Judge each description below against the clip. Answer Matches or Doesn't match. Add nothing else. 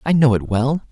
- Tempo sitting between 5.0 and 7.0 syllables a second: Matches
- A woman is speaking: Doesn't match